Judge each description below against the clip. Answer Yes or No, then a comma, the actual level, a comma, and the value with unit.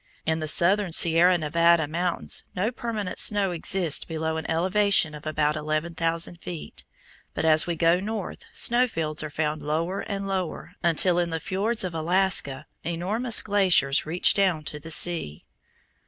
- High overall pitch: No, medium, 170 Hz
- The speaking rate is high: No, average, 160 wpm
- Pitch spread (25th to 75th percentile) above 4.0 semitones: No, average, 3.3 semitones